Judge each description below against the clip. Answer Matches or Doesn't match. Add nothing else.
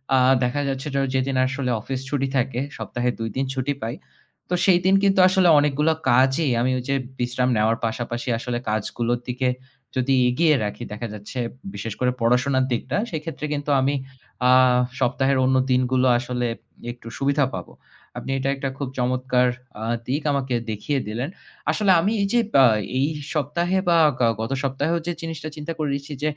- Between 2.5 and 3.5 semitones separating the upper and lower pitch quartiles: Matches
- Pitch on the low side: Matches